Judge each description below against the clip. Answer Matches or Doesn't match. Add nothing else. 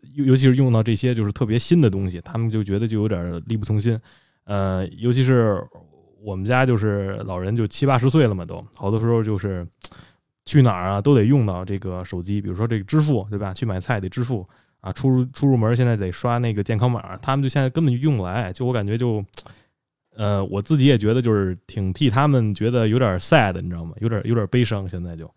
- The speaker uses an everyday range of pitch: Matches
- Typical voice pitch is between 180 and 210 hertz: Doesn't match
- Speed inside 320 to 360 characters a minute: Matches